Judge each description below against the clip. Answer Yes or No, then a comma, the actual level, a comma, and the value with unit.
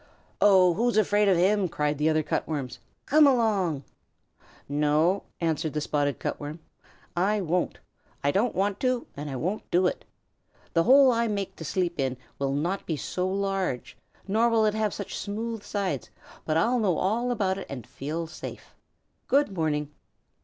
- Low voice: No, medium, 185 Hz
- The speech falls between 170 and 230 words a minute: Yes, average, 175 wpm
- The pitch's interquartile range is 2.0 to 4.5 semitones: No, wide, 5.5 semitones